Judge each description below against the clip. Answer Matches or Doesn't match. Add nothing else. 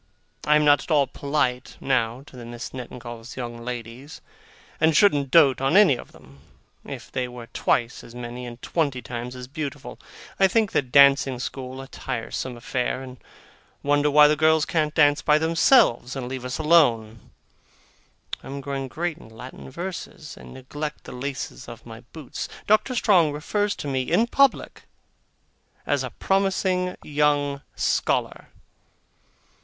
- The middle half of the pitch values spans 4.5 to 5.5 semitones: Doesn't match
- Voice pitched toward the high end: Doesn't match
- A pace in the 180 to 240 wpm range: Doesn't match